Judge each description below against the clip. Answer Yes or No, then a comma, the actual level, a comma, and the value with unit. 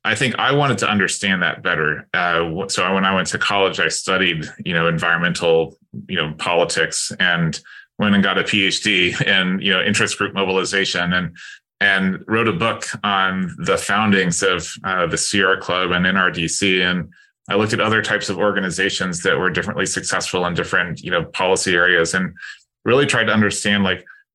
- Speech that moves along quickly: No, average, 180 wpm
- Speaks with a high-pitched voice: No, very low, 95 Hz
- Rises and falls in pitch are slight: Yes, narrow, 2.0 semitones